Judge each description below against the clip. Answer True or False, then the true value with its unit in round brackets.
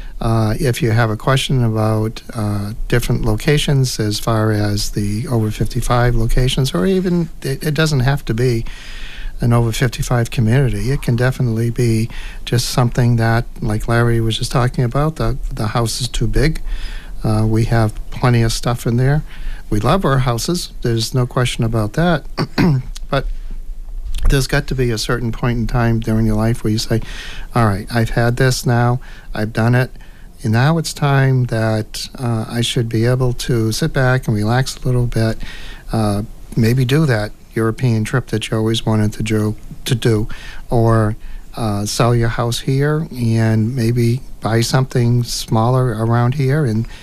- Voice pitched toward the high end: False (120 Hz)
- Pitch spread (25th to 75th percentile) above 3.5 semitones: False (2.6 semitones)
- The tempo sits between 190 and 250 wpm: False (175 wpm)